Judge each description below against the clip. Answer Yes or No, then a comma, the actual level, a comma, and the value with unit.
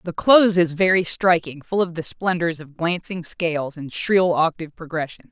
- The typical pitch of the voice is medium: Yes, medium, 170 Hz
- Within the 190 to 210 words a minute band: No, average, 180 wpm